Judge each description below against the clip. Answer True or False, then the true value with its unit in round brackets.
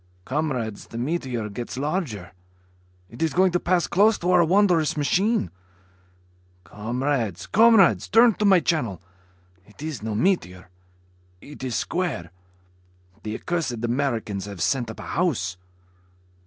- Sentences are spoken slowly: True (130 wpm)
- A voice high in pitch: False (140 Hz)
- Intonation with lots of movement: True (8.3 semitones)